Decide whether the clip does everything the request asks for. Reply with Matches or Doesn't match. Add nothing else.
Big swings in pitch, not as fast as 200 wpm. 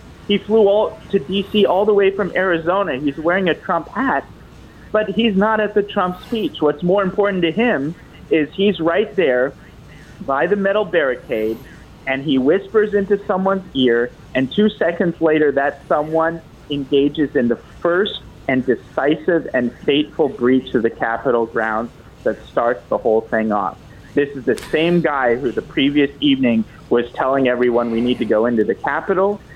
Matches